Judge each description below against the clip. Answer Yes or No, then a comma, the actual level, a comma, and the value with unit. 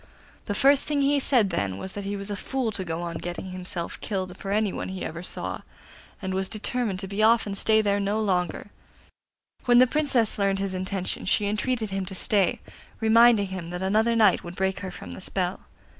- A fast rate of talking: Yes, fast, 210 wpm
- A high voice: Yes, high, 200 Hz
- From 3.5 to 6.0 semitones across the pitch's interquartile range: No, average, 2.8 semitones